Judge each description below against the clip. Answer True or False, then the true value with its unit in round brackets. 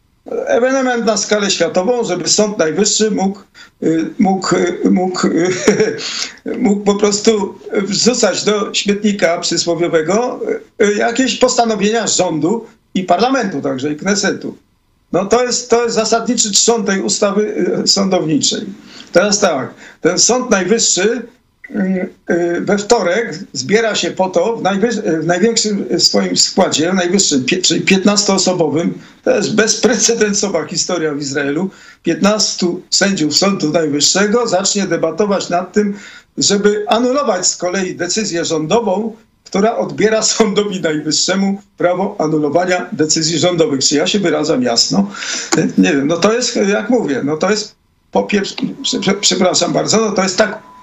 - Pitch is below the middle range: False (200 Hz)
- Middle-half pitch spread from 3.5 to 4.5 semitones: True (4.0 semitones)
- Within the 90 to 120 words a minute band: False (130 wpm)